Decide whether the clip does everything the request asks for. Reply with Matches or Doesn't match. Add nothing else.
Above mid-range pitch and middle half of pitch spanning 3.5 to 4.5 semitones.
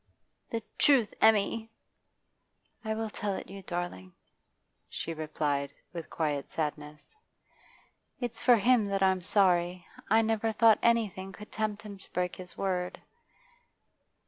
Matches